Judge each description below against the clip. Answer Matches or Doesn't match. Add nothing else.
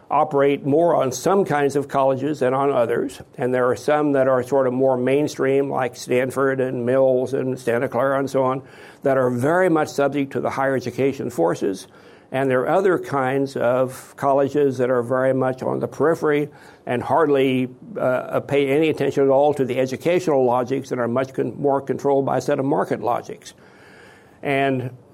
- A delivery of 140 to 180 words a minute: Doesn't match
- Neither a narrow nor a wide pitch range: Doesn't match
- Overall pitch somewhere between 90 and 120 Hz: Doesn't match